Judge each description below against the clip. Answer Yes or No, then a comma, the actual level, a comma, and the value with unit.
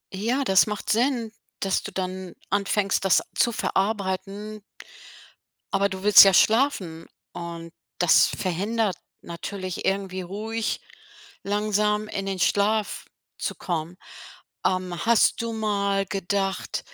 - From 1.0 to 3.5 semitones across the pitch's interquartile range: Yes, narrow, 2.4 semitones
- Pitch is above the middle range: Yes, high, 195 Hz